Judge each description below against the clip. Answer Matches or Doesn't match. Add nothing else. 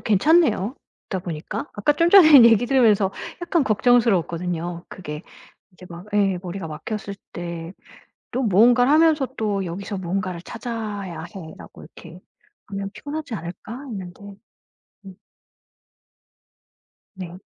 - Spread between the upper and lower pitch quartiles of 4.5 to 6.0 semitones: Matches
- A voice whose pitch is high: Matches